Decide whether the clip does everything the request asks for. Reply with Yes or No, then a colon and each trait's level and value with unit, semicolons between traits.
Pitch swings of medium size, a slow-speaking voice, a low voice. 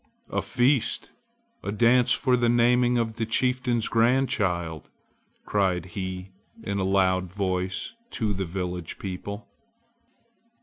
Yes: average, 4.6 semitones; slow, 120 wpm; low, 100 Hz